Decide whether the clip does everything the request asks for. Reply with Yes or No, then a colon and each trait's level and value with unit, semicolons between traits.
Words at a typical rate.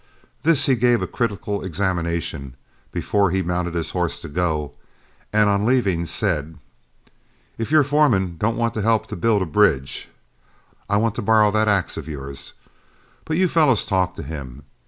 Yes: average, 165 wpm